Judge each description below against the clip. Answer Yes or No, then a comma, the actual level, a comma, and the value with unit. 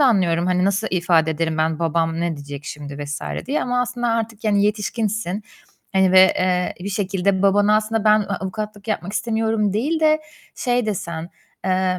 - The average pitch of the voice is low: No, high, 195 Hz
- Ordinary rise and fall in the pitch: Yes, average, 4.2 semitones